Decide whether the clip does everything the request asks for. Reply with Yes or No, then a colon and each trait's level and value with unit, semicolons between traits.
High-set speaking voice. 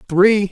Yes: high, 195 Hz